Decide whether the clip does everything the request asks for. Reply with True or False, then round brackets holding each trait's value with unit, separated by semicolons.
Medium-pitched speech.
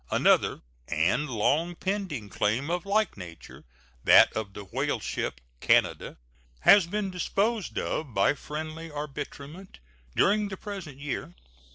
True (155 Hz)